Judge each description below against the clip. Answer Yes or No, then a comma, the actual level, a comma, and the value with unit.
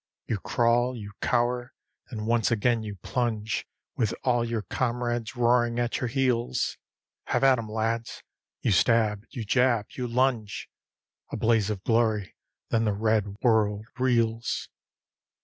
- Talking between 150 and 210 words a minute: No, average, 140 wpm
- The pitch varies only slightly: Yes, narrow, 2.0 semitones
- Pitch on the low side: Yes, low, 115 Hz